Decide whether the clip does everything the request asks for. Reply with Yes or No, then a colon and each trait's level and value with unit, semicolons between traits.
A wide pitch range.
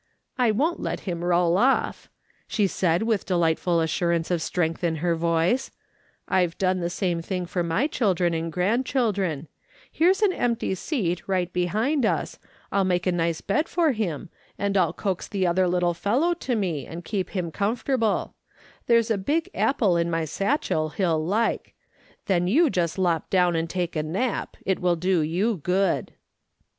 No: average, 4.4 semitones